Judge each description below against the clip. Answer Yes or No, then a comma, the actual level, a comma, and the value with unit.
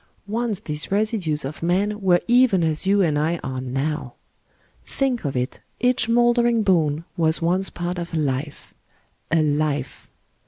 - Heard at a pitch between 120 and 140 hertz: No, medium, 170 Hz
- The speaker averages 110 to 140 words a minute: No, average, 160 wpm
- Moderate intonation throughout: No, wide, 5.8 semitones